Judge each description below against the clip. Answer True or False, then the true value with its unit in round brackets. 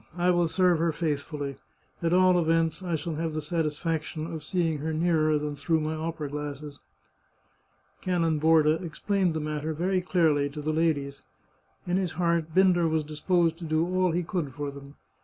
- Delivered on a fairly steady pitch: True (2.3 semitones)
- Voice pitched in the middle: True (160 Hz)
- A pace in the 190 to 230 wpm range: False (175 wpm)